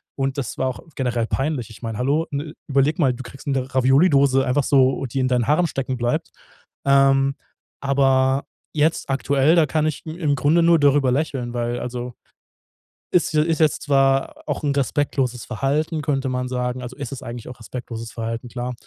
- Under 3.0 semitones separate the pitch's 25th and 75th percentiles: Yes, narrow, 2.5 semitones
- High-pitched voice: No, low, 135 Hz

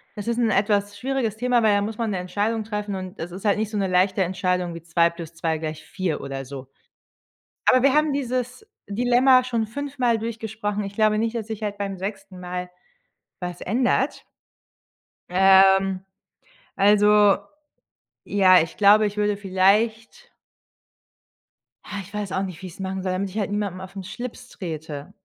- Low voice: No, high, 205 Hz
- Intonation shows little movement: No, average, 3.2 semitones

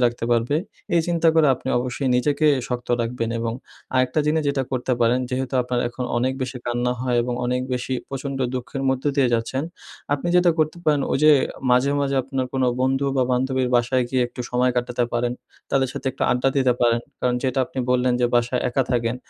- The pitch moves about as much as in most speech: No, narrow, 1.7 semitones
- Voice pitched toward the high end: No, low, 125 Hz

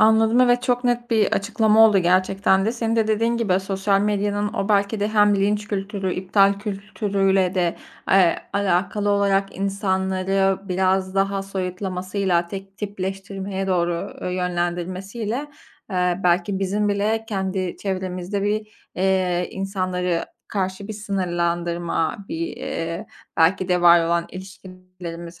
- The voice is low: No, high, 195 Hz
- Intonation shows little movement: Yes, narrow, 2.0 semitones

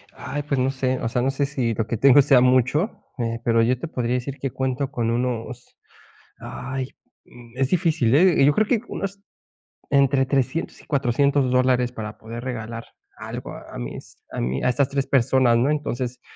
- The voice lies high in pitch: No, low, 130 Hz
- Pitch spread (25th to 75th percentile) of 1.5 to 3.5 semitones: Yes, narrow, 2.6 semitones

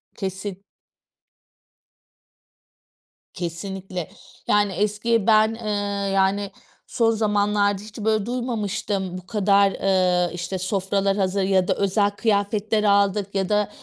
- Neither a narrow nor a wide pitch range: No, narrow, 1.6 semitones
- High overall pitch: Yes, high, 200 Hz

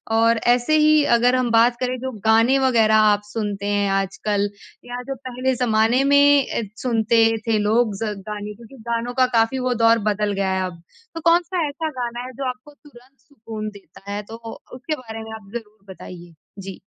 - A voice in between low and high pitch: No, high, 230 Hz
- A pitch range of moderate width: Yes, average, 3.4 semitones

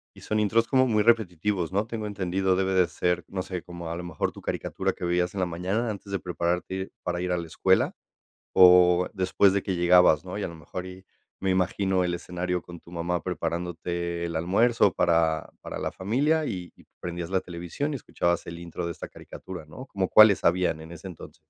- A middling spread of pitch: No, narrow, 2.0 semitones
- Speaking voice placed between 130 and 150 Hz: No, very low, 90 Hz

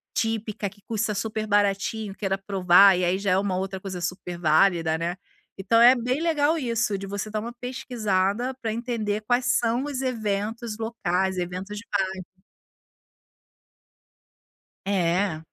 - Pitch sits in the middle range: No, high, 205 Hz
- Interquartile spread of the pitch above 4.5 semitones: No, average, 3.4 semitones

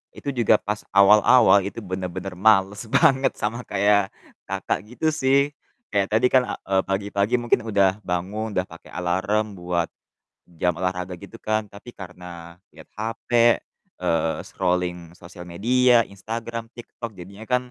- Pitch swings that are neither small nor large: Yes, average, 3.7 semitones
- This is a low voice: Yes, low, 100 Hz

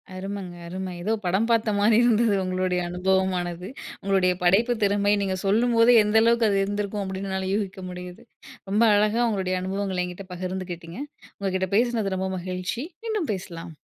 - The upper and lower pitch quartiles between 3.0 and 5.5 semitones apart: No, narrow, 2.5 semitones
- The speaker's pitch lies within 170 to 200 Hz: Yes, high, 195 Hz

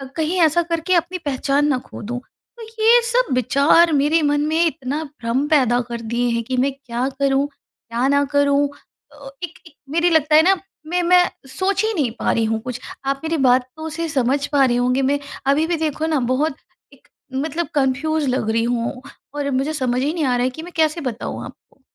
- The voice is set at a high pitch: Yes, very high, 285 Hz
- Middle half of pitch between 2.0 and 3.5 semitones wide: No, average, 3.9 semitones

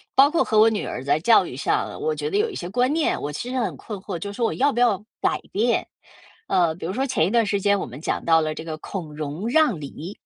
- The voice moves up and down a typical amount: No, wide, 7.4 semitones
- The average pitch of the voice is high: Yes, high, 205 Hz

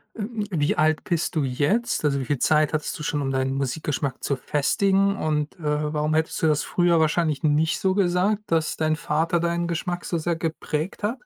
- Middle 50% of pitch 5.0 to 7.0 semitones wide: No, average, 2.8 semitones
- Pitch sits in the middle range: Yes, medium, 155 Hz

